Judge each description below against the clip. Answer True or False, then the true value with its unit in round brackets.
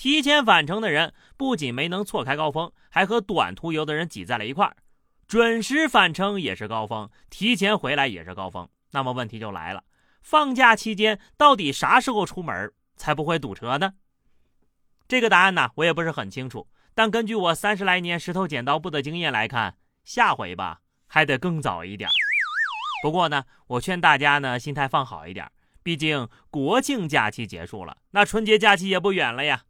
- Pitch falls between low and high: True (170 Hz)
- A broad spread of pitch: True (7.4 semitones)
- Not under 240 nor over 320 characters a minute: True (280 characters per minute)